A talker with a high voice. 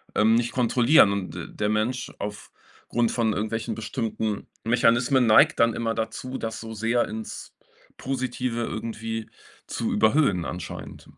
No: low, 115 Hz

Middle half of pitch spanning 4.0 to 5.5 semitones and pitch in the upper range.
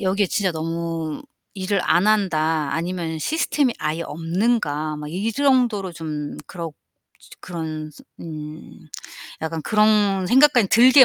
No: average, 5.1 semitones; medium, 175 Hz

